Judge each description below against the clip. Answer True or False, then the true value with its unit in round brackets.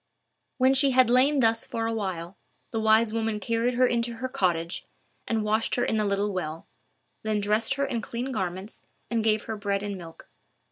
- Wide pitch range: False (2.9 semitones)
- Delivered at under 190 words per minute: False (195 wpm)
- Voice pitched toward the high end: True (220 Hz)